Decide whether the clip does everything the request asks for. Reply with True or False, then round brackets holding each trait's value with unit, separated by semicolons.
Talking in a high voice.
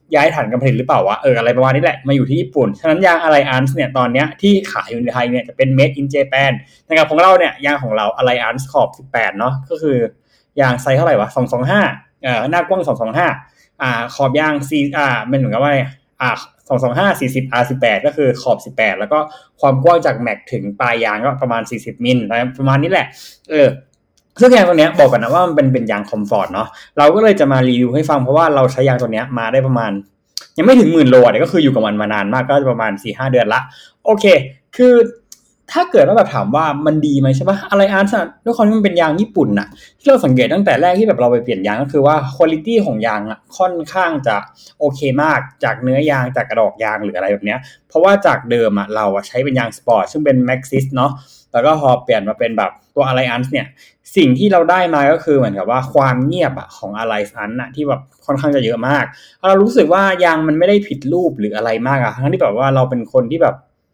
False (135 Hz)